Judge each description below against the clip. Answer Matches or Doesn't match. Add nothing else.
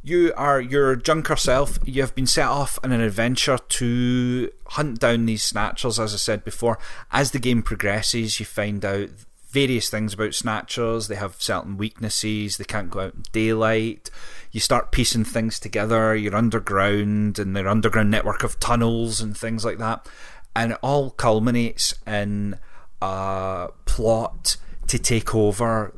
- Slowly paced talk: Doesn't match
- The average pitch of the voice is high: Doesn't match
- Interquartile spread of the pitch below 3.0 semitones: Matches